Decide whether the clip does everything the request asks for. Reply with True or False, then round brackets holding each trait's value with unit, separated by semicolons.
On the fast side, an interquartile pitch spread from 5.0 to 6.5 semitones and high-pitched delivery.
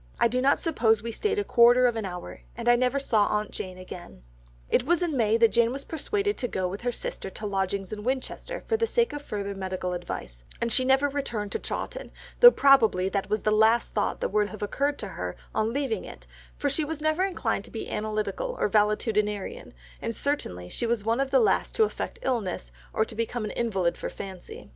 True (220 wpm; 5.3 semitones; 230 Hz)